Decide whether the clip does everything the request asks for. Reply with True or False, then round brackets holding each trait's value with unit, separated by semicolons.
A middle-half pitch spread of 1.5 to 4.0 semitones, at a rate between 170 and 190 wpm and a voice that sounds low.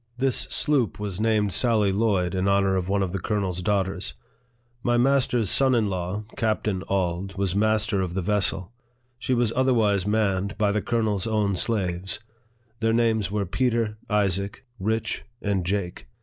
False (2.8 semitones; 160 wpm; 105 Hz)